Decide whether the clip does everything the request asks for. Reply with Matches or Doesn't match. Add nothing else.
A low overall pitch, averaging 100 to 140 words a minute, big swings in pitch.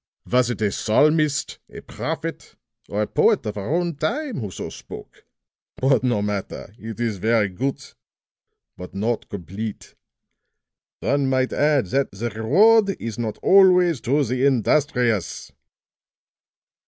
Matches